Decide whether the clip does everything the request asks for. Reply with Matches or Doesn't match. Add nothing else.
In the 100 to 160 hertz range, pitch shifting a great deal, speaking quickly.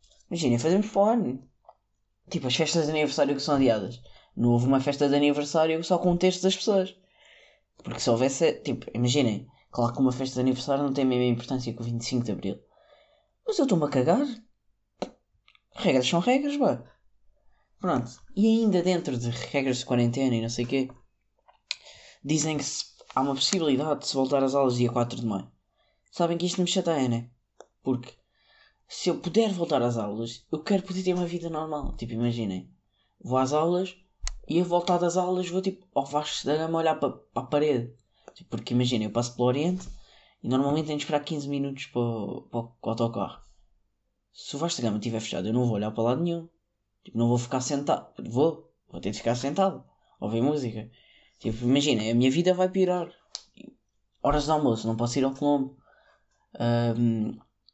Matches